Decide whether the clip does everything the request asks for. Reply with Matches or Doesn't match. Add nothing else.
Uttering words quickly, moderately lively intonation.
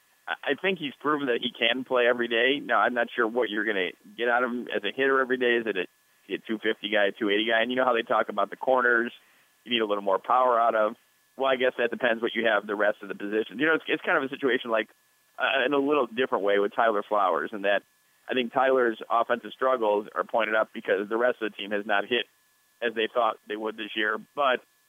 Matches